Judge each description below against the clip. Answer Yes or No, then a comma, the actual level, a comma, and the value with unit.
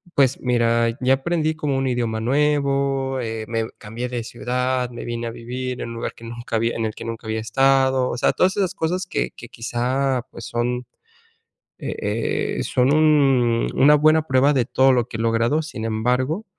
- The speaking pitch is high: No, low, 125 Hz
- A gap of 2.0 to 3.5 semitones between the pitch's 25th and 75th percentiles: Yes, average, 2.9 semitones